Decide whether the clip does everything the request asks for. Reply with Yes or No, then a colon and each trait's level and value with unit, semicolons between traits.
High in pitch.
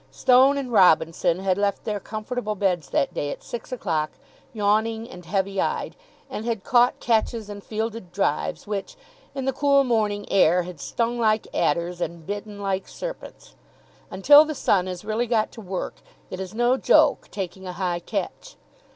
Yes: high, 205 Hz